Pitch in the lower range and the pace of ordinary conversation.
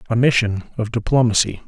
Yes: low, 115 Hz; average, 145 wpm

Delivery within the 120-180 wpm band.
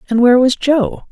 No: fast, 215 wpm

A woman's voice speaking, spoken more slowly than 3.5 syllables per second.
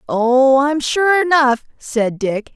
Yes: female; 3.1 syllables/s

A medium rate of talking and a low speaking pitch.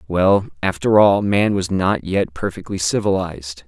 Yes: average, 145 wpm; very low, 95 Hz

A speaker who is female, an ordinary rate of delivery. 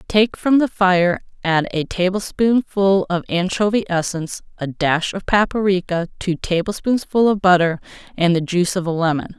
Yes: female; average, 155 wpm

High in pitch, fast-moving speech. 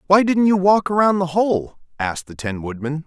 No: medium, 165 Hz; fast, 215 wpm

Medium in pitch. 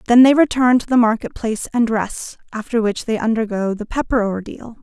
No: high, 230 Hz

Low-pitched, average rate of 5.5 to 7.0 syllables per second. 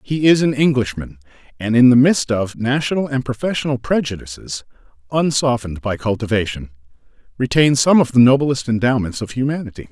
Yes: low, 125 Hz; 5.7 syllables/s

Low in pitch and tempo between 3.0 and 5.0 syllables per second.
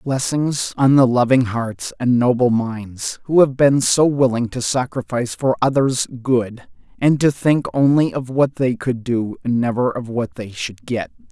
Yes: low, 125 Hz; 4.2 syllables/s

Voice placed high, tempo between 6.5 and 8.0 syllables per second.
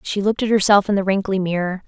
Yes: high, 195 Hz; 6.8 syllables/s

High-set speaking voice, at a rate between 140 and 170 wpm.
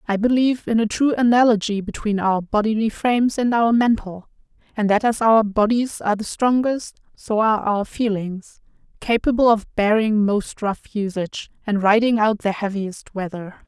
Yes: high, 215 Hz; average, 160 wpm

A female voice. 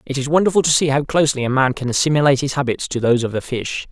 No: male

